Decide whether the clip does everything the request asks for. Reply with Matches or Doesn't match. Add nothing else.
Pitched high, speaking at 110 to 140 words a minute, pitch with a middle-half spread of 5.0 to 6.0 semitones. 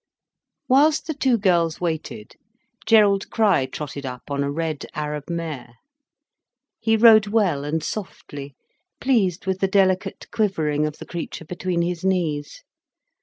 Doesn't match